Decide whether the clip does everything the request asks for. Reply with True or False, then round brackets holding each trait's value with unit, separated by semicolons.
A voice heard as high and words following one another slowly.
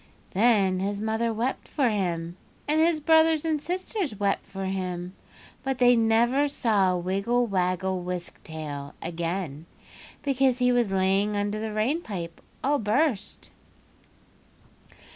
True (210 Hz; 130 wpm)